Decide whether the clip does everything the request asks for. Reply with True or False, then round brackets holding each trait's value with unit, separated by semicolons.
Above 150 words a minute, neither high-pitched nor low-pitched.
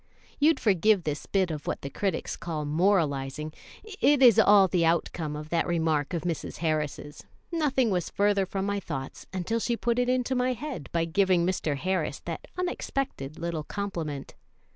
True (170 wpm; 180 Hz)